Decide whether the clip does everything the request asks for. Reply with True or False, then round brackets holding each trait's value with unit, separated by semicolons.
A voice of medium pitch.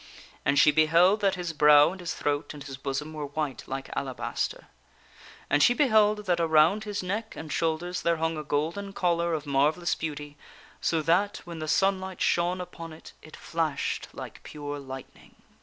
True (160 Hz)